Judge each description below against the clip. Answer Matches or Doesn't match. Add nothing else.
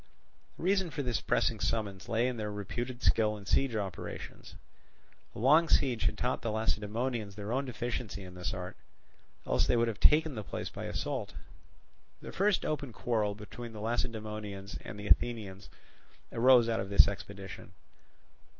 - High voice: Doesn't match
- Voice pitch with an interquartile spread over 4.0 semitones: Doesn't match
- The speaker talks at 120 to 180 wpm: Matches